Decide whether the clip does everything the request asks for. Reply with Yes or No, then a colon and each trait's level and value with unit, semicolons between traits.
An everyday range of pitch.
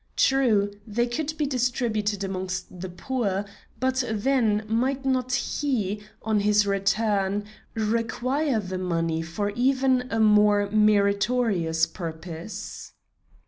Yes: average, 4.2 semitones